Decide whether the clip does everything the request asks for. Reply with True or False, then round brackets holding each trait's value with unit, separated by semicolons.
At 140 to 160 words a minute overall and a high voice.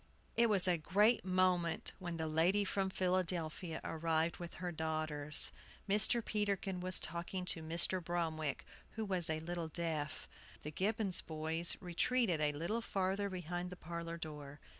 False (150 wpm; 175 Hz)